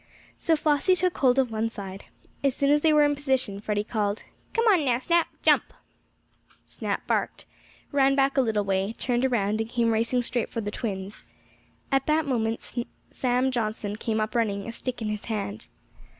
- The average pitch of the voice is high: Yes, high, 235 Hz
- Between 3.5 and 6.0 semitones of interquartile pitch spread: Yes, average, 4.1 semitones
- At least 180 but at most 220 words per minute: Yes, average, 185 wpm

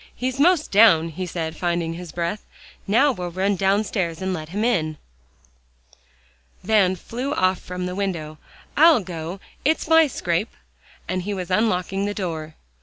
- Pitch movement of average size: Yes, average, 4.0 semitones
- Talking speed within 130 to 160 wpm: Yes, average, 155 wpm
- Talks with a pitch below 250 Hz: Yes, medium, 185 Hz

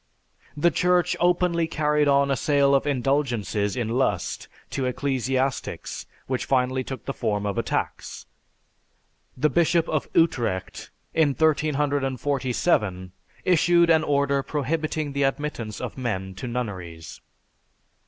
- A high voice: No, medium, 140 Hz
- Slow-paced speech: Yes, slow, 125 wpm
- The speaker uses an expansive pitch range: No, average, 3.7 semitones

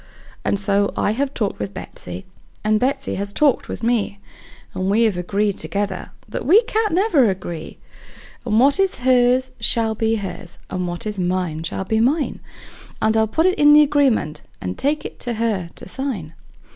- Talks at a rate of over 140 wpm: Yes, average, 185 wpm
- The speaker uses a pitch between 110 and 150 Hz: No, high, 220 Hz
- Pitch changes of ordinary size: No, wide, 5.9 semitones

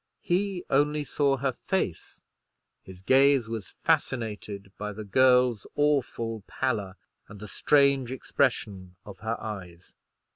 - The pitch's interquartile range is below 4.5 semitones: No, average, 5.3 semitones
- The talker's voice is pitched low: Yes, low, 115 Hz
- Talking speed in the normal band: No, slow, 120 wpm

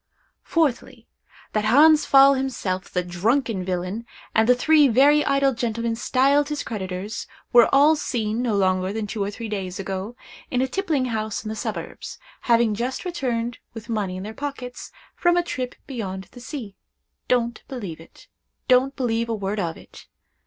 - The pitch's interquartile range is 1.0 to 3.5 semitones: No, average, 4.7 semitones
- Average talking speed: Yes, average, 165 wpm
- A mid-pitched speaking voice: No, high, 235 Hz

